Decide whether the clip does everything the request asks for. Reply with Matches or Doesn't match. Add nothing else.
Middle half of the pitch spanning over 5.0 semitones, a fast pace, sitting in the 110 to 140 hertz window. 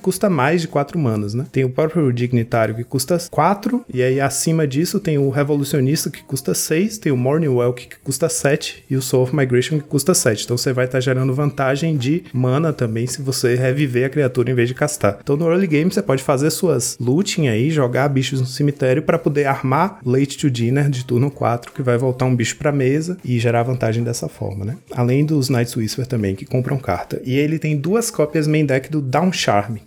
Doesn't match